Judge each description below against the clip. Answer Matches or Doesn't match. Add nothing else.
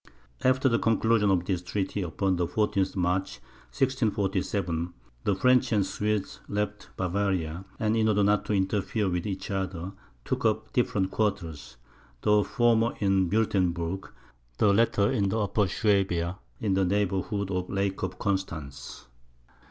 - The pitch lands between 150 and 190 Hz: Doesn't match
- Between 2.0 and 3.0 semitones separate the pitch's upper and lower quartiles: Matches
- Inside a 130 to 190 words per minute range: Matches